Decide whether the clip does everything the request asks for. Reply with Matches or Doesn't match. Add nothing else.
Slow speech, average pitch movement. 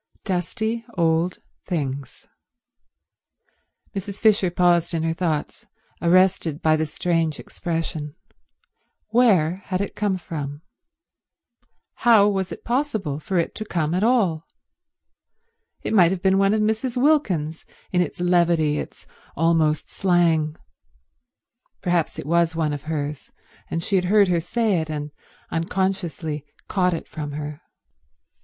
Matches